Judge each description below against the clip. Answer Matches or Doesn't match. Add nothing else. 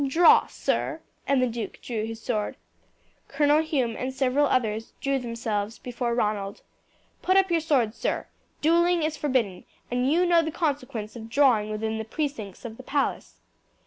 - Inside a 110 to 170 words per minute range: Matches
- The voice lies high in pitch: Matches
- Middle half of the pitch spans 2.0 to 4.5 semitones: Doesn't match